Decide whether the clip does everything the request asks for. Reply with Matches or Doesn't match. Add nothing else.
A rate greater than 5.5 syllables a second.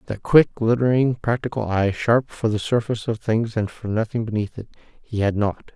Doesn't match